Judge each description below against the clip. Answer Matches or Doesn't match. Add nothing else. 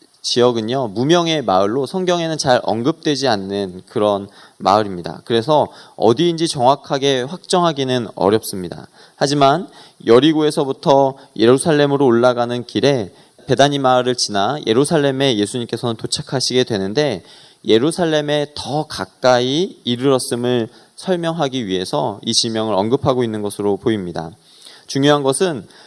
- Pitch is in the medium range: Doesn't match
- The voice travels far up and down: Doesn't match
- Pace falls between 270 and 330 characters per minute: Matches